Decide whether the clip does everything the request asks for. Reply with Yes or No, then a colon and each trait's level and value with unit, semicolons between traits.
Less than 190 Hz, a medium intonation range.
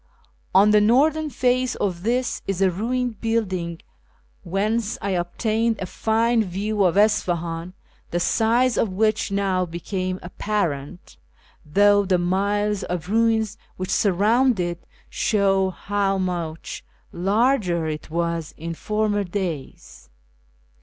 No: high, 200 Hz; average, 3.8 semitones